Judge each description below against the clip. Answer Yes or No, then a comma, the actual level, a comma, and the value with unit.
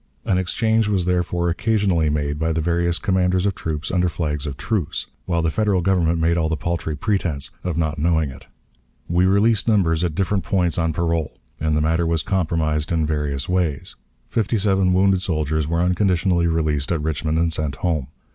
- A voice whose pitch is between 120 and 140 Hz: No, very low, 85 Hz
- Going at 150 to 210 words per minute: Yes, average, 185 wpm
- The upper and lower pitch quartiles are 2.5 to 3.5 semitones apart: Yes, average, 2.9 semitones